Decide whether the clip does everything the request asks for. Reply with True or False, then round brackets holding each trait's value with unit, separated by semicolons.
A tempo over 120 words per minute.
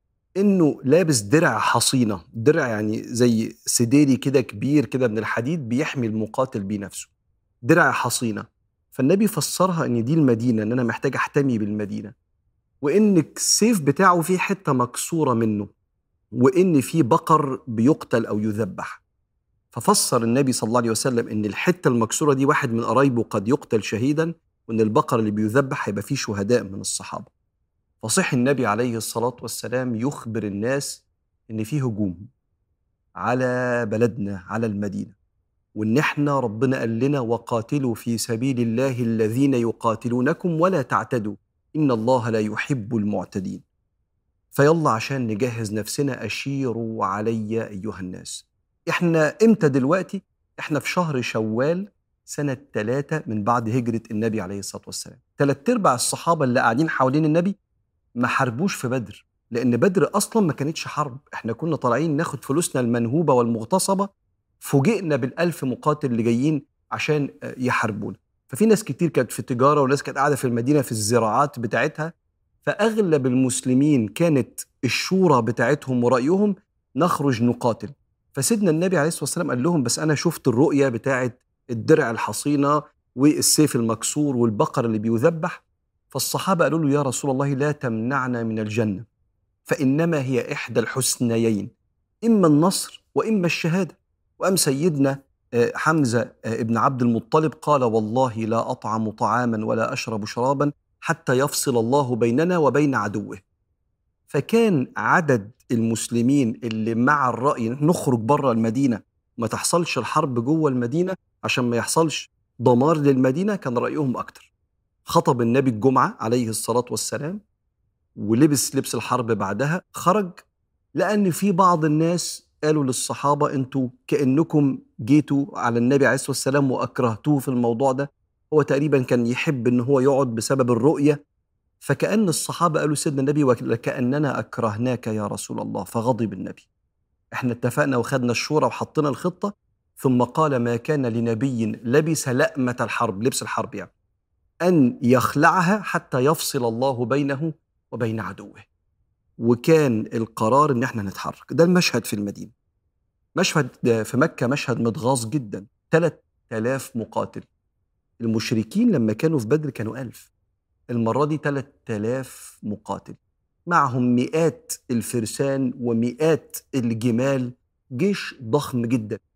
True (130 wpm)